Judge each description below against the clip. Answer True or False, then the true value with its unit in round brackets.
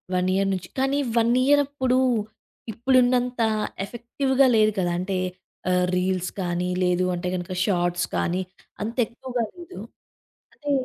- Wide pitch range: True (6.1 semitones)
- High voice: True (215 Hz)